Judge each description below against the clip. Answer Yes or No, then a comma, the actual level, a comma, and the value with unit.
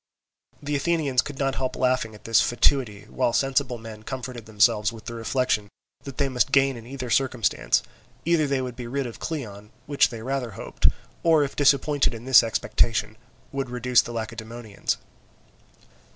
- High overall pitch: No, low, 125 Hz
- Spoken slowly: No, average, 165 wpm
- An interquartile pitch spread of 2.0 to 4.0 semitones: Yes, average, 3.2 semitones